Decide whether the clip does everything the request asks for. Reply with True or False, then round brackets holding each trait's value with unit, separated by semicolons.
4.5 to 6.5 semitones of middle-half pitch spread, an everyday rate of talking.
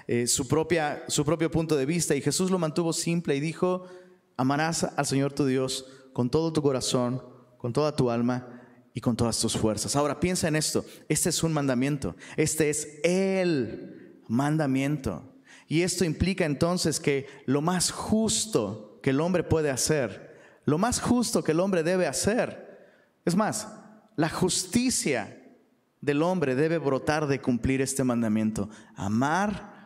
True (5.1 semitones; 160 wpm)